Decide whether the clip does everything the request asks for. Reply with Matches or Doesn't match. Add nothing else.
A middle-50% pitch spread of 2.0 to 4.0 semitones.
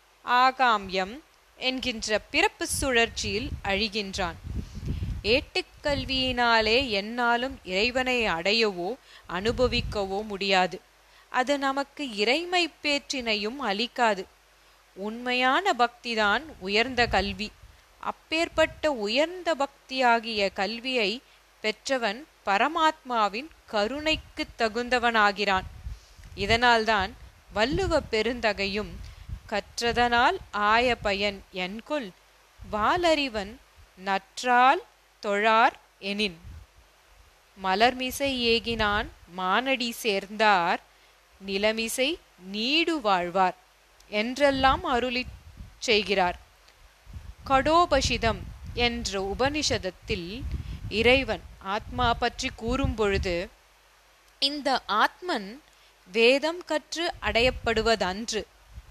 Doesn't match